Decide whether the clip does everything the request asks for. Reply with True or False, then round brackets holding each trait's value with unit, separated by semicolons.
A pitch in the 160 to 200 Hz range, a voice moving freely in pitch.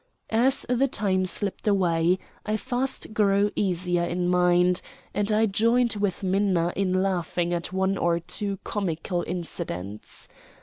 False (190 Hz; 2.8 semitones)